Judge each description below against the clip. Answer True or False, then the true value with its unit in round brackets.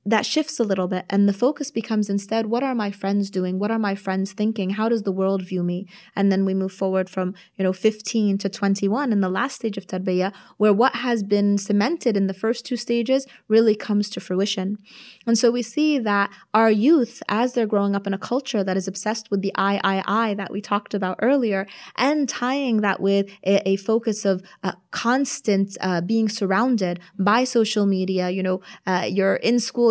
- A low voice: False (205 Hz)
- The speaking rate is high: True (215 wpm)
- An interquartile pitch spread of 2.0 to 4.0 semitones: True (3.0 semitones)